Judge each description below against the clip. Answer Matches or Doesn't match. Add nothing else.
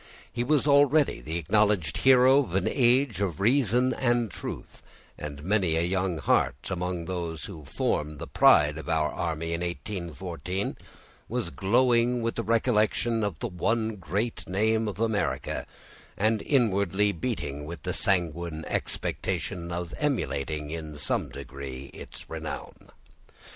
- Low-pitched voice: Matches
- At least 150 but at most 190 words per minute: Doesn't match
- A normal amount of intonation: Doesn't match